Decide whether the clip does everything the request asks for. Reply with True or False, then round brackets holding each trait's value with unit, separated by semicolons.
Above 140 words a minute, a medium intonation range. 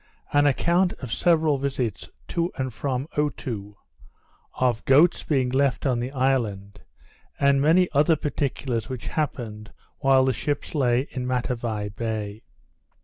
False (135 wpm; 3.5 semitones)